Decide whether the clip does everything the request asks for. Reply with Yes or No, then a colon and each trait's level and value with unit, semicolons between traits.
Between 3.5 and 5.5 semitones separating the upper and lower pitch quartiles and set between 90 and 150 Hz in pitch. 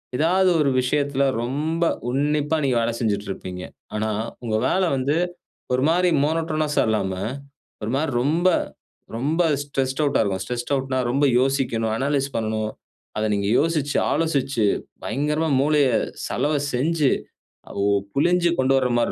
Yes: average, 4.4 semitones; medium, 140 Hz